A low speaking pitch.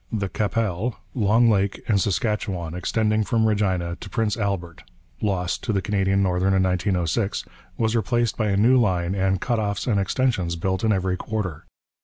Yes: low, 100 Hz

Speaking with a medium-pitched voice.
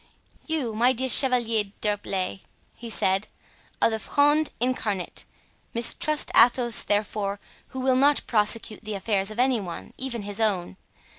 No: high, 225 Hz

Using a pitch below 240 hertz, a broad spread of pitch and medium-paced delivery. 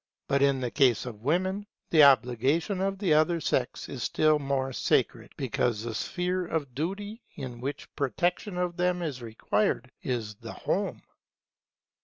Yes: medium, 140 Hz; wide, 6.2 semitones; average, 155 wpm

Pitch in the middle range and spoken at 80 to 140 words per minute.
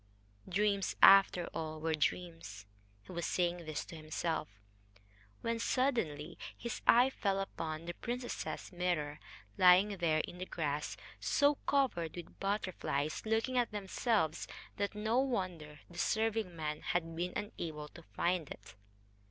Yes: medium, 180 Hz; slow, 135 wpm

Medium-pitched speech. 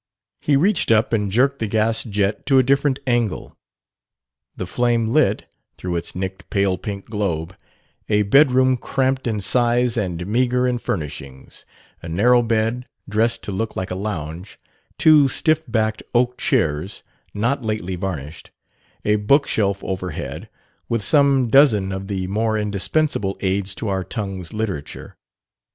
No: low, 110 Hz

